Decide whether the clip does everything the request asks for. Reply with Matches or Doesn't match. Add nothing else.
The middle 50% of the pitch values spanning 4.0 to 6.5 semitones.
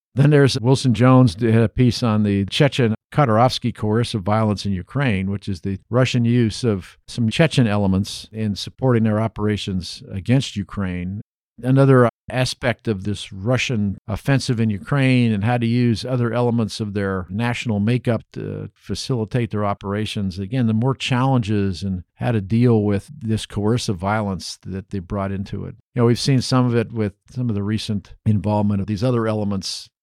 Doesn't match